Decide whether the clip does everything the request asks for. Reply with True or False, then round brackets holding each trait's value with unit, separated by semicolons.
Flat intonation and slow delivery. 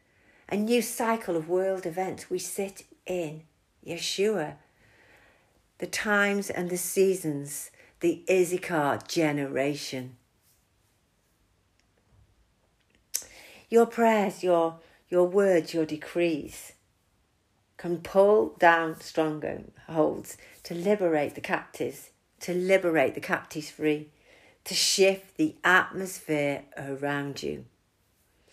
False (4.9 semitones; 95 wpm)